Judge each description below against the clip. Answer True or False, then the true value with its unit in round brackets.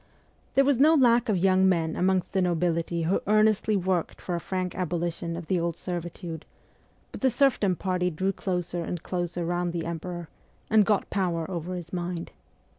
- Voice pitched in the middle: True (180 Hz)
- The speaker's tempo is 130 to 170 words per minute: False (180 wpm)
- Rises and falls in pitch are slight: True (2.1 semitones)